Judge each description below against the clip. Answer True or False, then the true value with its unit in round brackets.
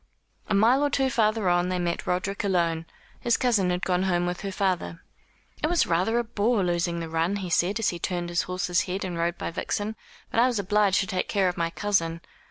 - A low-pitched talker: False (185 Hz)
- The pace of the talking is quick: True (230 wpm)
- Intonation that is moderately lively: True (3.3 semitones)